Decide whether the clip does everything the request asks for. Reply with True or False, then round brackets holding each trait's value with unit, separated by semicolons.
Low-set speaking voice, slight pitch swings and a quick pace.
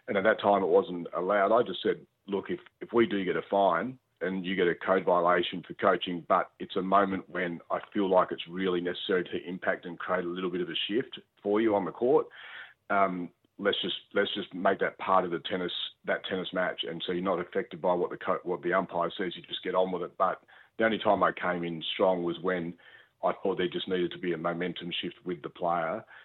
True (90 Hz; 1.5 semitones; 245 wpm)